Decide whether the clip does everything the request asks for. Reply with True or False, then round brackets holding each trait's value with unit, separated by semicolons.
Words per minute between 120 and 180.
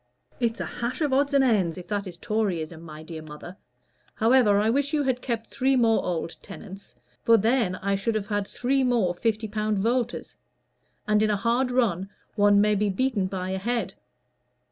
False (190 wpm)